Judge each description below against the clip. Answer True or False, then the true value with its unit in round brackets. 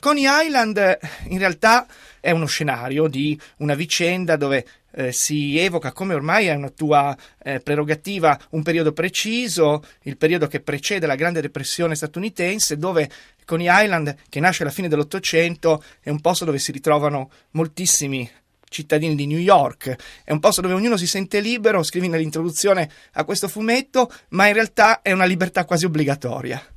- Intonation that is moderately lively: True (4.1 semitones)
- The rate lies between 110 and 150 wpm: False (160 wpm)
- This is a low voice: False (165 Hz)